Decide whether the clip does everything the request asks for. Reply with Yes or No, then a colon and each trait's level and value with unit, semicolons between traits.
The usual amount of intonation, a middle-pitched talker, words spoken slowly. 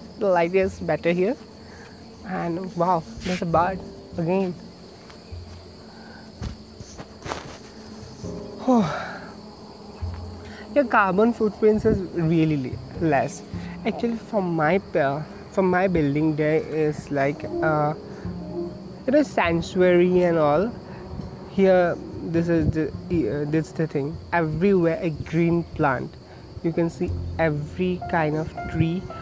Yes: average, 3.8 semitones; medium, 170 Hz; slow, 110 wpm